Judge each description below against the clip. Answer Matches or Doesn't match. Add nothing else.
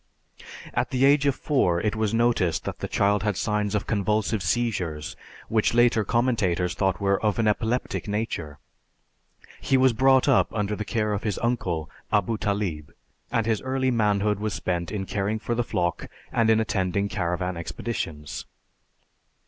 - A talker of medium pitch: Doesn't match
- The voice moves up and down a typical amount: Matches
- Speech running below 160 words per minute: Doesn't match